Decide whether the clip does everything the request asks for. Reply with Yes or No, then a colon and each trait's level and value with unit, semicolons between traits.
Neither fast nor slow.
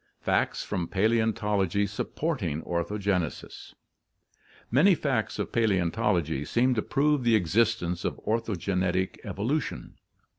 No: slow, 105 wpm